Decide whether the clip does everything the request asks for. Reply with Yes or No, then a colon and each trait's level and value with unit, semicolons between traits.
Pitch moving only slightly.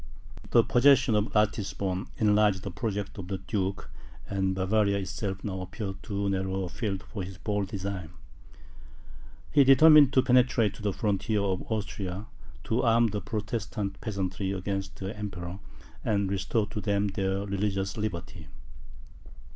Yes: narrow, 2.1 semitones